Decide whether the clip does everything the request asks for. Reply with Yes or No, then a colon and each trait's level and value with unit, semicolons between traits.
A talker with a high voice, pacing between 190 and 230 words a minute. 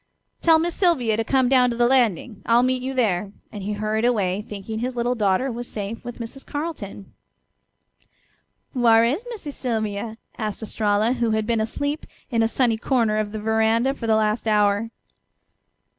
No: high, 230 Hz; average, 175 wpm